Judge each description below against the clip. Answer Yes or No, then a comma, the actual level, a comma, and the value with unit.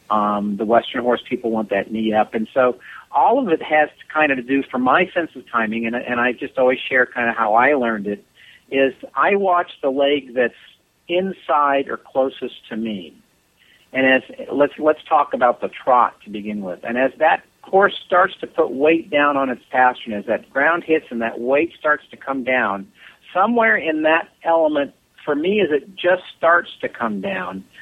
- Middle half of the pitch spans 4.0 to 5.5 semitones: Yes, average, 4.8 semitones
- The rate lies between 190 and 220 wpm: Yes, fast, 205 wpm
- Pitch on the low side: Yes, low, 130 Hz